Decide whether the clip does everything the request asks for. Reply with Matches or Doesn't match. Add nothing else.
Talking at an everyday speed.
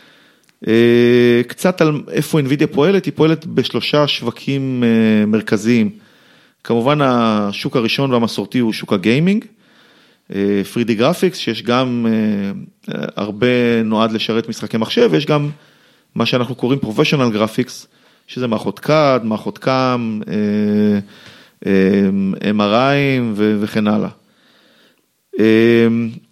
Doesn't match